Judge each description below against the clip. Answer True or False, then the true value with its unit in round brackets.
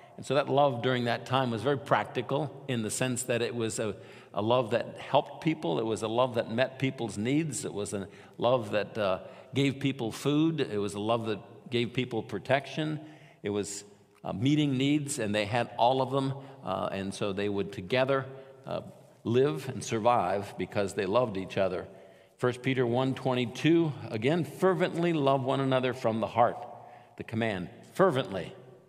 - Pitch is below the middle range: True (125 Hz)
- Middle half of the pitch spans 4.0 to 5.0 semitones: True (4.4 semitones)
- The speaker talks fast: False (185 wpm)